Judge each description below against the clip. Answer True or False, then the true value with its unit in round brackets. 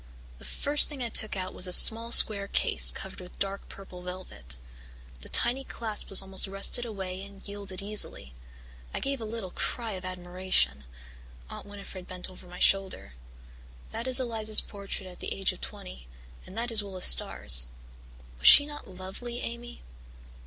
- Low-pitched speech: False (195 Hz)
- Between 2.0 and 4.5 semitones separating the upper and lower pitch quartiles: True (3.7 semitones)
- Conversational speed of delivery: True (170 wpm)